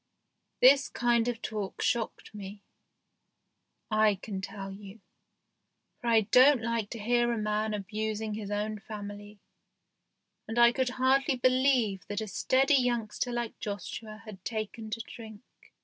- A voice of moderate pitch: No, high, 220 Hz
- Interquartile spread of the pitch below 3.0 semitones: Yes, narrow, 2.5 semitones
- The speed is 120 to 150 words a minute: Yes, average, 140 wpm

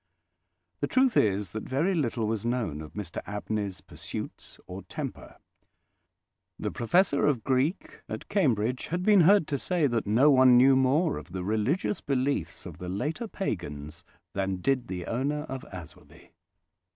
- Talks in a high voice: No, low, 125 Hz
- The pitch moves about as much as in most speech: No, wide, 6.6 semitones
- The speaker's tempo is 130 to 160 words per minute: Yes, average, 155 wpm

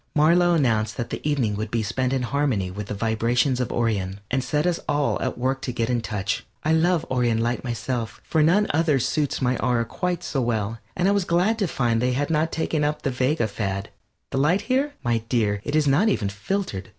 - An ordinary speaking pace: No, fast, 225 wpm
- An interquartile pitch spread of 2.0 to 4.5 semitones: No, average, 5.3 semitones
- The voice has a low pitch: Yes, low, 130 Hz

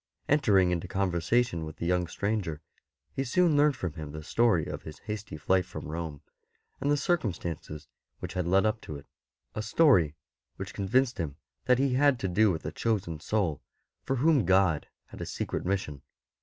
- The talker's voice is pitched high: No, very low, 95 Hz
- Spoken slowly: No, average, 190 wpm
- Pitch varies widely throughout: Yes, wide, 6.7 semitones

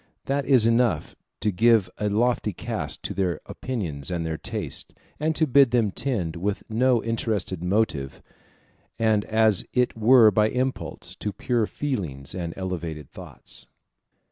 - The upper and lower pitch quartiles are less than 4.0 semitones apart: No, average, 5.3 semitones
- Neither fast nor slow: Yes, average, 145 wpm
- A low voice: Yes, low, 110 Hz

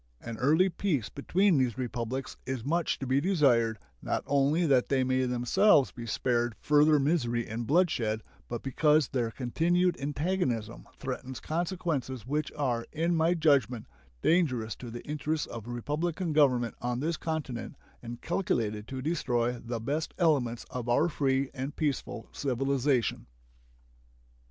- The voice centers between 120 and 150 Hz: Yes, low, 135 Hz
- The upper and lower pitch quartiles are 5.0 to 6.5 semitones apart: No, average, 4.6 semitones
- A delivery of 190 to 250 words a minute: No, average, 140 wpm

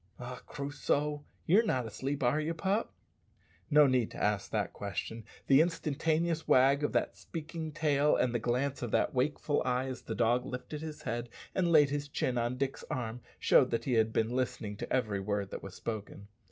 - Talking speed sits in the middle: Yes, average, 195 wpm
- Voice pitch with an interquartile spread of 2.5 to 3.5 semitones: No, average, 3.9 semitones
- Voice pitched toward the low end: Yes, low, 130 Hz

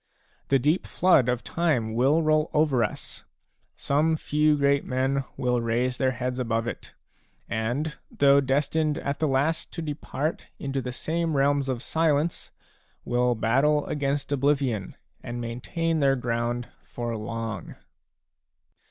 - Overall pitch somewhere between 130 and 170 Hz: Yes, low, 135 Hz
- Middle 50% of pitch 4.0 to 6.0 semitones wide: No, average, 3.6 semitones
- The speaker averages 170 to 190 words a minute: No, average, 140 wpm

